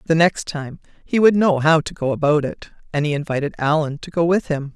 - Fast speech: Yes, fast, 240 wpm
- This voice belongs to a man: No, female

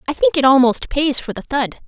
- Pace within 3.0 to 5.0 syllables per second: No, 5.3 syllables/s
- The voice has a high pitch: Yes, very high, 280 Hz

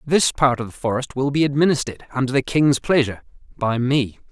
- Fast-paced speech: No, average, 195 wpm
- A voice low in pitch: Yes, low, 130 Hz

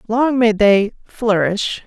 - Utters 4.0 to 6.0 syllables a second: No, 3.2 syllables/s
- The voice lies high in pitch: Yes, high, 220 Hz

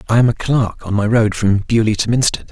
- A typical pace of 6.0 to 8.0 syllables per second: No, 5.6 syllables/s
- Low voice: Yes, low, 110 Hz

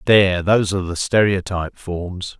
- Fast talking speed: No, average, 150 wpm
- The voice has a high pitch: No, very low, 95 Hz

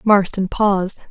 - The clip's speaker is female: Yes, female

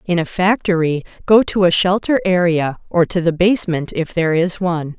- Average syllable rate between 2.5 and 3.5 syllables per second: No, 5.2 syllables/s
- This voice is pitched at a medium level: Yes, medium, 175 Hz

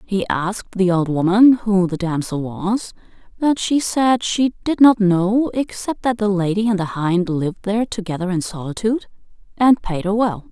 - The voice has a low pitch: No, high, 200 Hz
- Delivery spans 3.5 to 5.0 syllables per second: Yes, 4.7 syllables/s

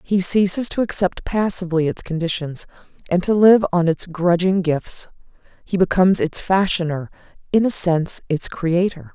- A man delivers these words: No, female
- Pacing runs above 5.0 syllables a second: No, 4.9 syllables/s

